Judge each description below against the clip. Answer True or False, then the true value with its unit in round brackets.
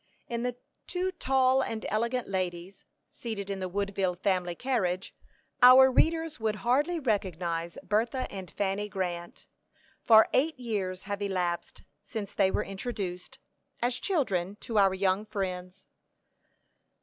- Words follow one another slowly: True (130 wpm)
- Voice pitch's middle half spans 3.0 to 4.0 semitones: False (4.8 semitones)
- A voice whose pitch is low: False (200 Hz)